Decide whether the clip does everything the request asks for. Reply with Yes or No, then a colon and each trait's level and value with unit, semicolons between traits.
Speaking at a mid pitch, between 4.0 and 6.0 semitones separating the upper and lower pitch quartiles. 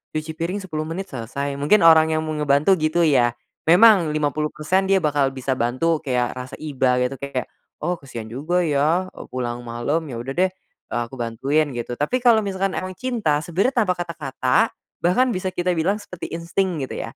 Yes: medium, 155 Hz; average, 5.1 semitones